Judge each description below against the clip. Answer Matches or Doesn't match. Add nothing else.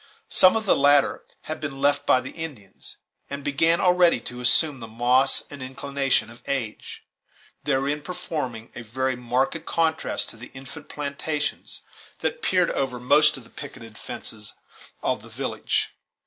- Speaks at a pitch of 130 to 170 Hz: Matches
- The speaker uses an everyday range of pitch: Matches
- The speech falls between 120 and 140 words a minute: Doesn't match